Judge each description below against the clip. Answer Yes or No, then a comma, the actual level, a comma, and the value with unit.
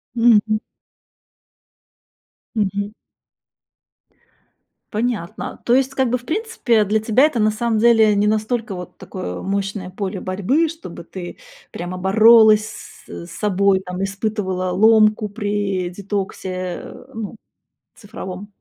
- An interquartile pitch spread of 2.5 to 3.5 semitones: Yes, average, 2.9 semitones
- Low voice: No, high, 210 Hz